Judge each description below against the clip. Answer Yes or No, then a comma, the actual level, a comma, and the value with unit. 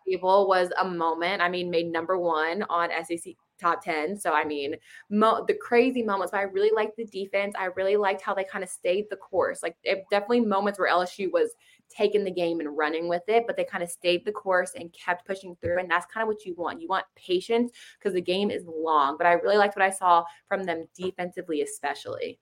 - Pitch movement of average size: Yes, average, 3.2 semitones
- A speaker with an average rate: No, fast, 230 wpm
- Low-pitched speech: No, high, 190 Hz